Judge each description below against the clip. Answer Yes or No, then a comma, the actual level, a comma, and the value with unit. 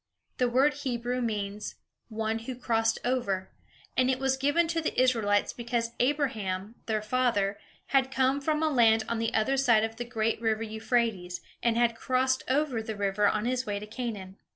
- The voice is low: No, high, 235 Hz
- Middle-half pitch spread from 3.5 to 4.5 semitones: No, average, 3.1 semitones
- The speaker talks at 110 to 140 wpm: No, average, 180 wpm